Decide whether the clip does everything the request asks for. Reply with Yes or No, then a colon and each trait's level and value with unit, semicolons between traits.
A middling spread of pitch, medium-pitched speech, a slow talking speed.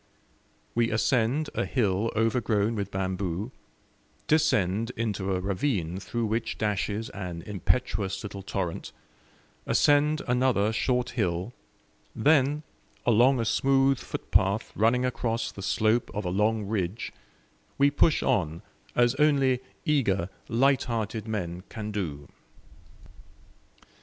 No: average, 4.2 semitones; low, 110 Hz; slow, 110 wpm